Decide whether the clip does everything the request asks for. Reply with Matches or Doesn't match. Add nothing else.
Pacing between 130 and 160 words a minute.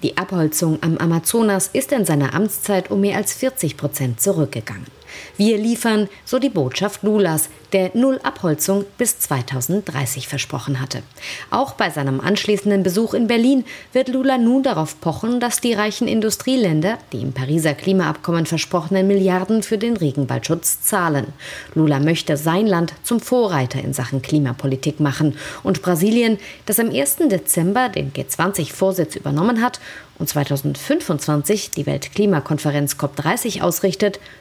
Matches